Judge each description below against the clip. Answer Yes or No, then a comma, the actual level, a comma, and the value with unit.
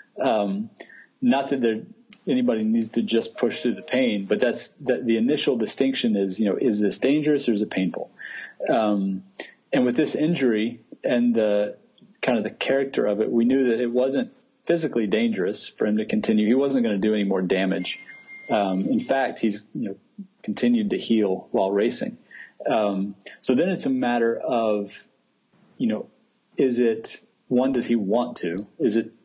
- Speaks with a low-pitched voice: Yes, low, 120 Hz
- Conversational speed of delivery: Yes, average, 185 wpm